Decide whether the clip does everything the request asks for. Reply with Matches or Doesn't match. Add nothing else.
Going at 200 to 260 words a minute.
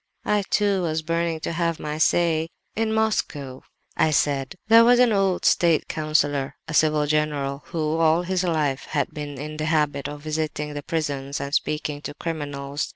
Doesn't match